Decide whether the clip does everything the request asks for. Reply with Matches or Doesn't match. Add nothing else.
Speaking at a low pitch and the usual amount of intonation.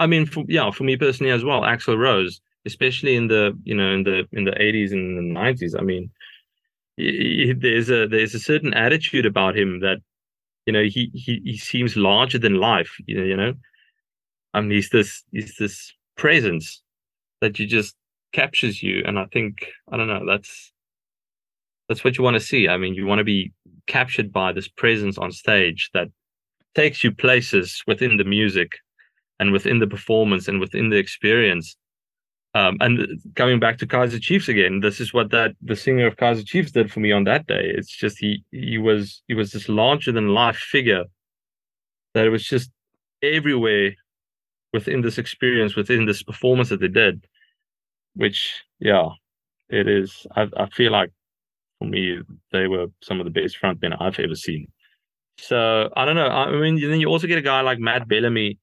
Matches